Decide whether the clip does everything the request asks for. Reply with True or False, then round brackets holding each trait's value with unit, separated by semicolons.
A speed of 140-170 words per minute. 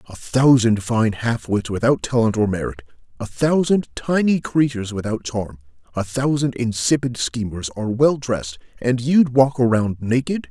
True (155 wpm)